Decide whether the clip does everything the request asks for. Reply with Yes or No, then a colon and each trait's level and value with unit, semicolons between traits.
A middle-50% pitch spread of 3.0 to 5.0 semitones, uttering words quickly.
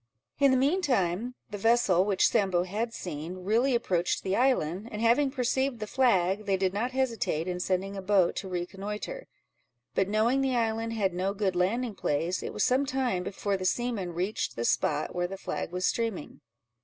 No: average, 4.7 semitones; average, 190 wpm